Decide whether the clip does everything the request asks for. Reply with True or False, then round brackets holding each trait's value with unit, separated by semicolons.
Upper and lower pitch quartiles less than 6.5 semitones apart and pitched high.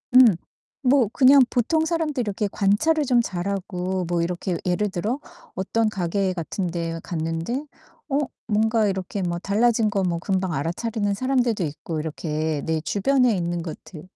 True (5.4 semitones; 195 Hz)